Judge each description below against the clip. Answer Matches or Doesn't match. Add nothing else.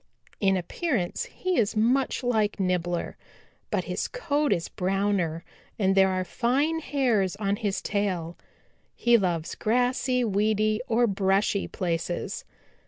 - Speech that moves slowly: Matches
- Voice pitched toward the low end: Doesn't match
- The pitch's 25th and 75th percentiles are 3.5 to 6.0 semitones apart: Matches